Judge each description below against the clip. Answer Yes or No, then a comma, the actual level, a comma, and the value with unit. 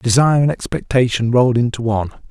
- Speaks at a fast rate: No, average, 155 wpm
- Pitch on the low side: Yes, low, 120 Hz